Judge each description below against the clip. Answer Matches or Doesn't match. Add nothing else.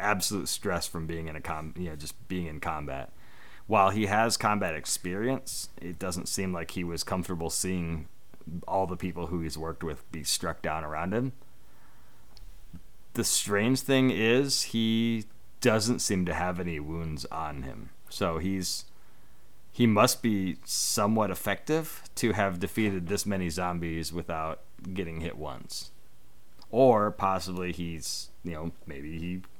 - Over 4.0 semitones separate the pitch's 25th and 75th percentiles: Matches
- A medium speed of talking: Matches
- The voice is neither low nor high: Doesn't match